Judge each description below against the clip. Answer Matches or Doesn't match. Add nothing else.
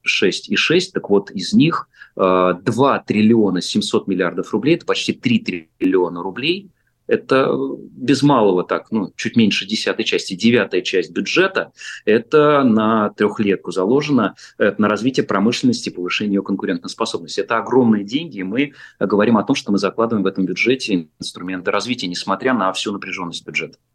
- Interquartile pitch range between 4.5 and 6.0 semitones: Matches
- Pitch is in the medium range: Doesn't match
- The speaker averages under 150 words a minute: Doesn't match